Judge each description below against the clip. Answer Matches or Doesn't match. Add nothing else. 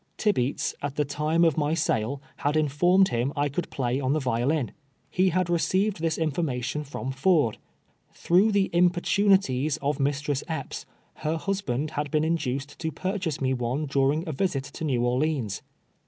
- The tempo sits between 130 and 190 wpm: Matches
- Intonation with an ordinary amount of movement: Matches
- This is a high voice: Doesn't match